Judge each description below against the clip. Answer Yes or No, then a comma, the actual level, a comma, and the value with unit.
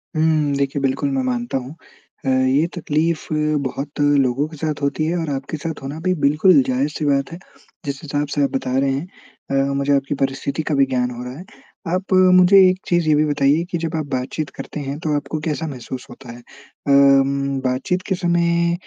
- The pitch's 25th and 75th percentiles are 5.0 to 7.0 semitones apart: No, average, 3.0 semitones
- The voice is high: No, medium, 145 Hz